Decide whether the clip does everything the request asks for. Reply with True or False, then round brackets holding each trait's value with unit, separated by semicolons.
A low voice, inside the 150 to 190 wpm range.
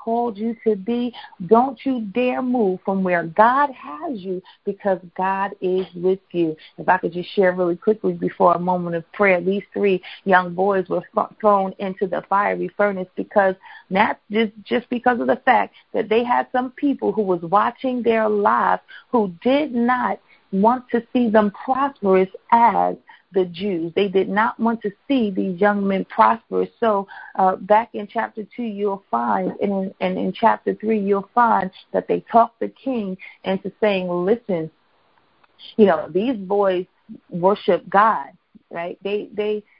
False (205 Hz; 170 wpm)